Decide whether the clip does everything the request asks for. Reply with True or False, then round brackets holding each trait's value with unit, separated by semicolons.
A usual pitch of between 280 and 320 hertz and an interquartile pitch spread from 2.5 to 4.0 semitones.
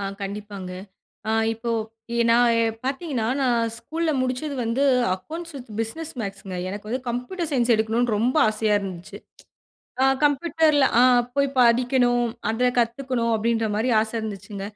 False (240 Hz; 3.6 semitones)